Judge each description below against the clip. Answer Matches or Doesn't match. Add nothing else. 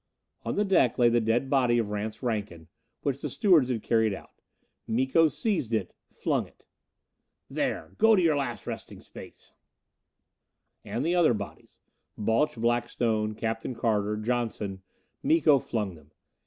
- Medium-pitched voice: Doesn't match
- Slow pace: Doesn't match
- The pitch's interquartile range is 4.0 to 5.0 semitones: Matches